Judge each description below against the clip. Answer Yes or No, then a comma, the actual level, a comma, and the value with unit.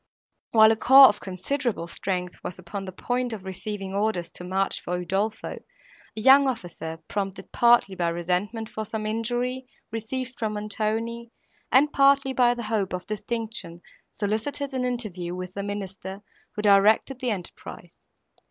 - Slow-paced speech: No, average, 150 wpm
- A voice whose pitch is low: No, high, 215 Hz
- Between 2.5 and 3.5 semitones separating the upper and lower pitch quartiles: No, average, 4.1 semitones